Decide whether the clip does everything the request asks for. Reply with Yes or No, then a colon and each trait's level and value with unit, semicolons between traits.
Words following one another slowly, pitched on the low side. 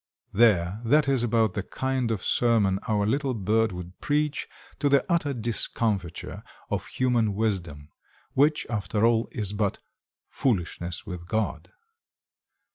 Yes: slow, 130 wpm; low, 110 Hz